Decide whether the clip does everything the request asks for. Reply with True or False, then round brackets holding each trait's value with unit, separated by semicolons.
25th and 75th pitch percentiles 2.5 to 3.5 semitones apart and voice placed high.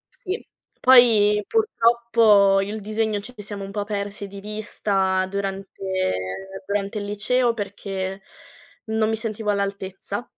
False (1.9 semitones; 205 Hz)